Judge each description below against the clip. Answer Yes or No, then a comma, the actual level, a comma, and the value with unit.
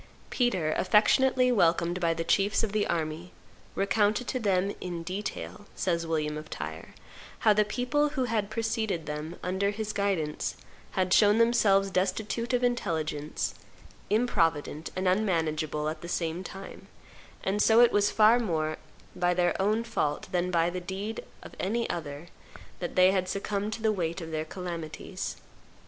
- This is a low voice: No, high, 190 Hz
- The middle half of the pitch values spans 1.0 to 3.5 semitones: No, average, 4.4 semitones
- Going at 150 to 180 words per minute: Yes, average, 160 wpm